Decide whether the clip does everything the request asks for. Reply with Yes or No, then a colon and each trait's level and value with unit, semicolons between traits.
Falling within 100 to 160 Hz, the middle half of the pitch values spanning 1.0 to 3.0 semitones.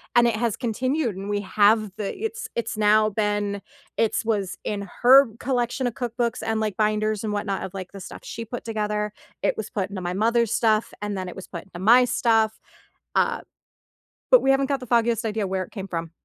No: high, 215 Hz; average, 2.7 semitones